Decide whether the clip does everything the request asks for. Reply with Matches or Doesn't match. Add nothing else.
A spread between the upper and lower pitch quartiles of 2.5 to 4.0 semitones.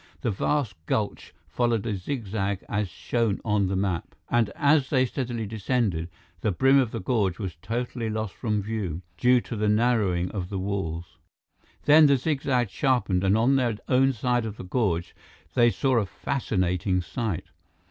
Doesn't match